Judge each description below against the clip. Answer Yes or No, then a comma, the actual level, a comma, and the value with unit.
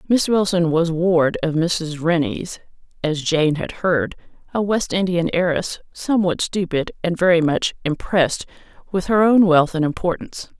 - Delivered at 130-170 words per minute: Yes, average, 155 wpm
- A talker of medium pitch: Yes, medium, 170 Hz